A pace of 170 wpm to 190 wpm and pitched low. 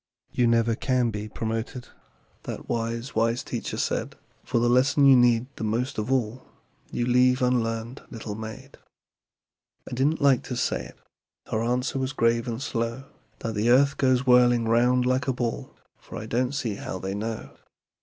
Yes: average, 175 wpm; low, 120 Hz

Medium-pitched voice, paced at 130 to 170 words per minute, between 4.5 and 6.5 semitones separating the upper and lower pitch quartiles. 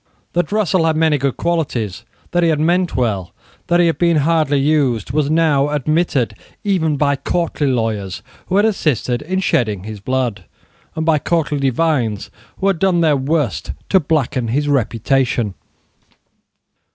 Yes: medium, 150 Hz; average, 155 wpm; average, 5.0 semitones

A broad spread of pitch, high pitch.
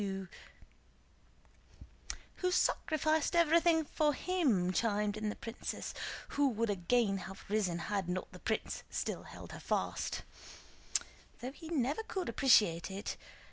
Yes: wide, 7.8 semitones; high, 235 Hz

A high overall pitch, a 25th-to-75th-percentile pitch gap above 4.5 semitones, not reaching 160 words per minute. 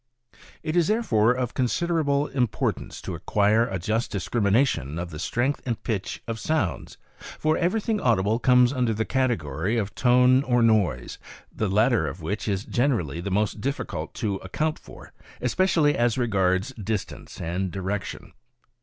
No: low, 115 Hz; average, 5.2 semitones; average, 150 wpm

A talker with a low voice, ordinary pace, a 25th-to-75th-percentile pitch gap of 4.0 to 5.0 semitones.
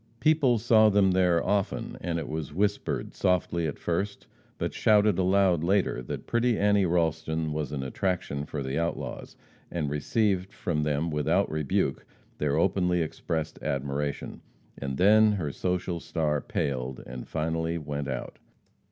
Yes: very low, 85 Hz; average, 145 wpm; average, 4.5 semitones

